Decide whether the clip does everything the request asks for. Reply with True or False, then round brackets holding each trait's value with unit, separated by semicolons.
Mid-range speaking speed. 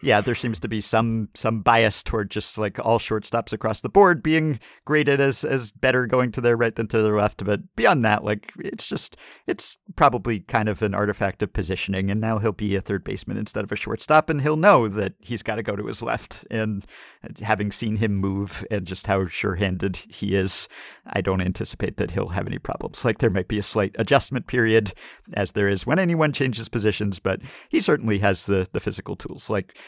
False (220 wpm)